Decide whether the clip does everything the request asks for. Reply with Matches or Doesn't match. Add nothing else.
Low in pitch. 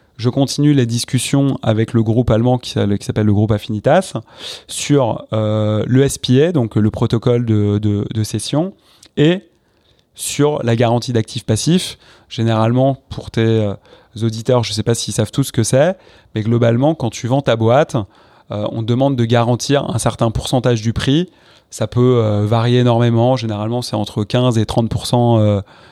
Matches